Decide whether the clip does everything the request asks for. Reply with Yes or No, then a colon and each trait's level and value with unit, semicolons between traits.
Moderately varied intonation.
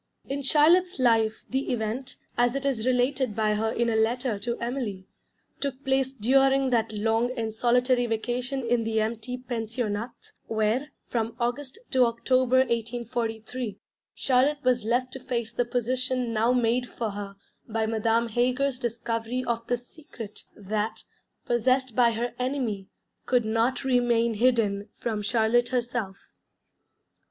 No: narrow, 2.3 semitones